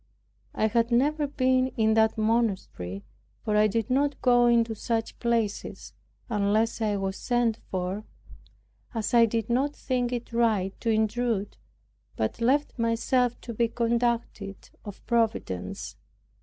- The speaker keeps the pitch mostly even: Yes, narrow, 2.2 semitones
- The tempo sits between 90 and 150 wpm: Yes, slow, 135 wpm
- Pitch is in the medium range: No, high, 230 Hz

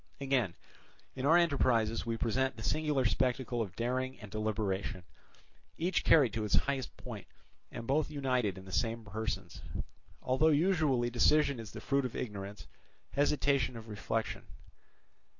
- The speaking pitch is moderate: No, low, 125 Hz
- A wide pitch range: No, average, 4.1 semitones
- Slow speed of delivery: No, average, 145 wpm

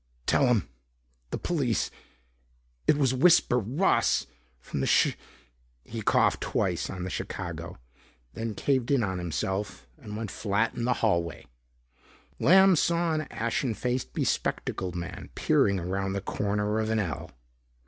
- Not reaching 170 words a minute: Yes, average, 150 wpm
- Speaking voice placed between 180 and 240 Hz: No, low, 110 Hz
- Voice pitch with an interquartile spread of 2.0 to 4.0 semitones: No, average, 5.2 semitones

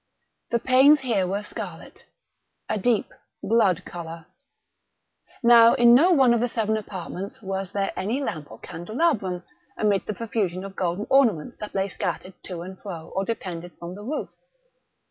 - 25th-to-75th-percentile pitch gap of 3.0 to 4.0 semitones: No, average, 4.4 semitones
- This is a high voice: Yes, high, 200 Hz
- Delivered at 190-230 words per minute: No, average, 155 wpm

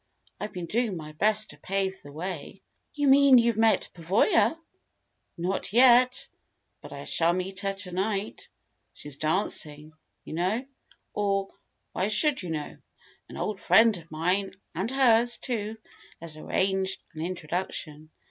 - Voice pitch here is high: Yes, high, 195 Hz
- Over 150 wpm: No, average, 145 wpm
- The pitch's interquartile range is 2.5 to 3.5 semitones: No, average, 4.8 semitones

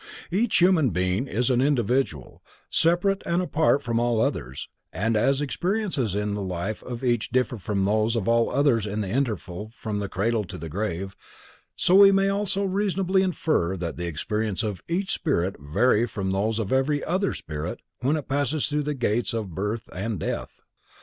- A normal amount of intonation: No, wide, 6.9 semitones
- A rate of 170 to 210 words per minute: Yes, average, 185 wpm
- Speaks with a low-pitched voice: Yes, low, 115 Hz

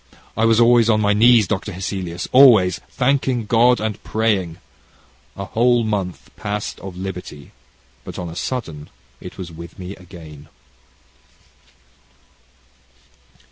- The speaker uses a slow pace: Yes, slow, 125 wpm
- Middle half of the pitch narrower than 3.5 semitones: No, average, 4.3 semitones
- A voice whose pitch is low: Yes, low, 100 Hz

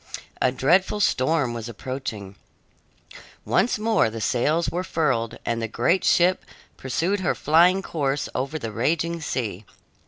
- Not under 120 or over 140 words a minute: Yes, slow, 135 wpm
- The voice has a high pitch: No, medium, 145 Hz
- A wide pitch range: Yes, wide, 6.4 semitones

